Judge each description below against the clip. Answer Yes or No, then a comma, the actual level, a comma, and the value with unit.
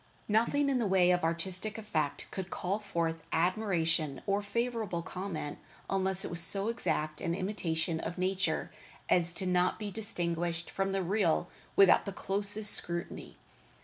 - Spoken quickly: No, average, 150 wpm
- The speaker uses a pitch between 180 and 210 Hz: Yes, medium, 185 Hz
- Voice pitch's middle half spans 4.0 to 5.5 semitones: No, average, 3.3 semitones